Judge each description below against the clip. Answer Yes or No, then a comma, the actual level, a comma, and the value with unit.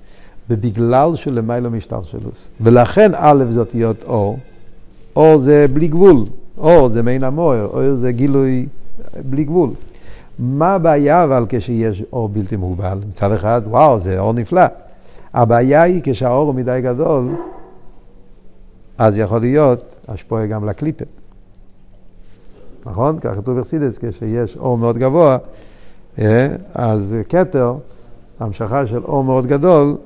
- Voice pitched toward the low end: Yes, low, 120 Hz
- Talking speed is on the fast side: No, average, 125 wpm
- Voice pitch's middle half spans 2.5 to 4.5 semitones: Yes, average, 4.2 semitones